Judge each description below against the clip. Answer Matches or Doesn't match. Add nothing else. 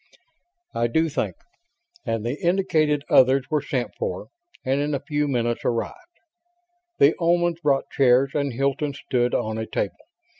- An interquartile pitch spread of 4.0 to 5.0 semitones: Doesn't match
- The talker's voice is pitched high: Doesn't match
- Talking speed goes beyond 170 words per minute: Doesn't match